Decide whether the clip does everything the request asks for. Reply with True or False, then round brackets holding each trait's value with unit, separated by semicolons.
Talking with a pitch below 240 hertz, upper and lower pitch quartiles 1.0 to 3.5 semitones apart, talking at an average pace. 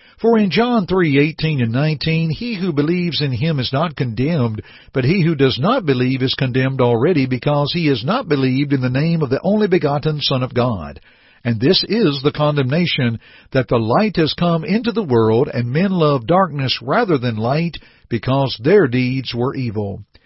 False (140 Hz; 4.8 semitones; 190 wpm)